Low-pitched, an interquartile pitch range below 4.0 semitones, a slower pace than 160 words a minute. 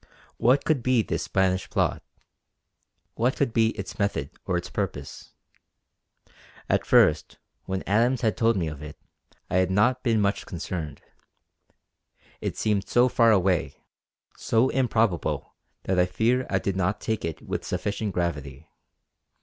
No: low, 100 Hz; average, 4.3 semitones; average, 145 wpm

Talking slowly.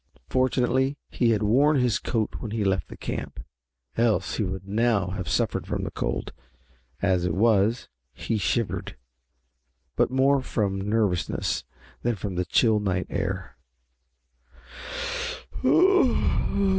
Yes: slow, 125 wpm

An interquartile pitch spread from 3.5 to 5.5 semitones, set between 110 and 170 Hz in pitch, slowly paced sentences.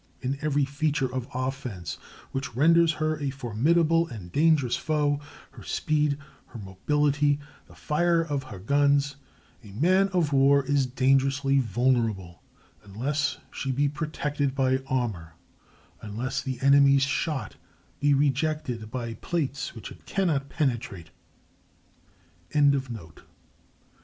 No: average, 2.9 semitones; medium, 140 Hz; slow, 110 wpm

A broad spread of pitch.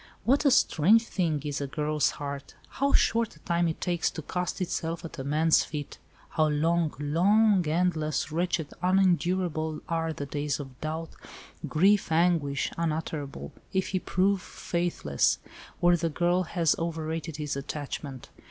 No: average, 3.1 semitones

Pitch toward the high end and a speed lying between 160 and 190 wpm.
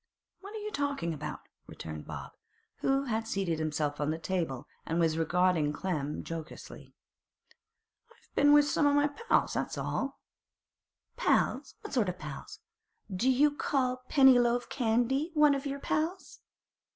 No: high, 235 Hz; average, 140 wpm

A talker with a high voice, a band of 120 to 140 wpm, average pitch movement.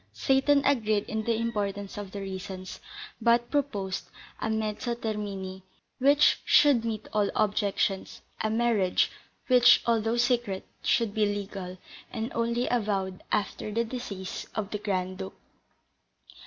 Yes: high, 215 Hz; slow, 135 wpm; average, 3.1 semitones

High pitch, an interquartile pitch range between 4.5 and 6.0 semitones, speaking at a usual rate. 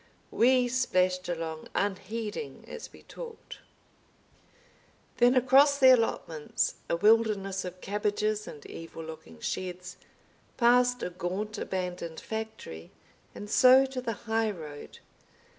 No: high, 210 Hz; average, 5.2 semitones; slow, 115 wpm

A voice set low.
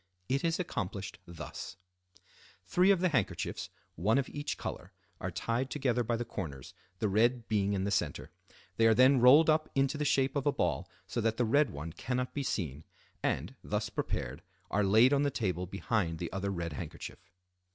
Yes: low, 115 Hz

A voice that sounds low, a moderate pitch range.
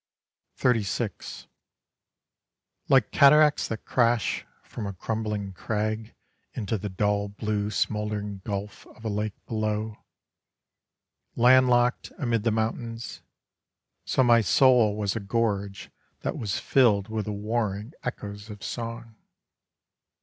No: low, 110 Hz; narrow, 2.3 semitones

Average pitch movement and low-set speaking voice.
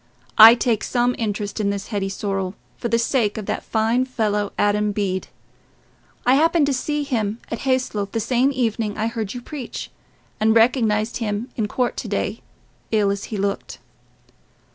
No: average, 3.0 semitones; high, 220 Hz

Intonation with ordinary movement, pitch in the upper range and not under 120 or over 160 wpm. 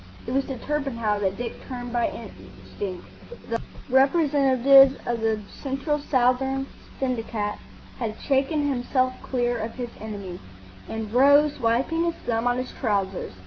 Yes: average, 3.2 semitones; very high, 250 Hz; average, 140 wpm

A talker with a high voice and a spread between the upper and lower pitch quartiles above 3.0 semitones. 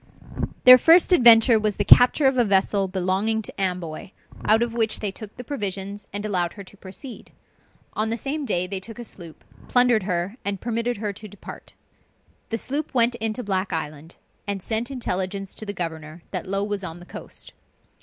Yes: high, 205 Hz; average, 3.7 semitones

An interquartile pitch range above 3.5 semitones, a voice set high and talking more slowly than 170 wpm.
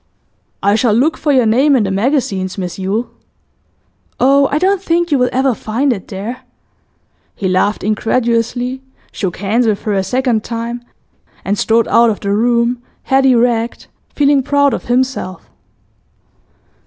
Yes: average, 4.0 semitones; high, 235 Hz; average, 155 wpm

